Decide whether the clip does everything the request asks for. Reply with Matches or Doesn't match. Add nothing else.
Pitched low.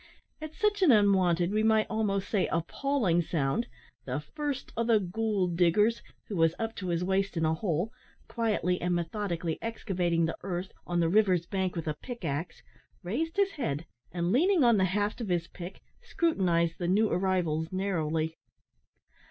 Doesn't match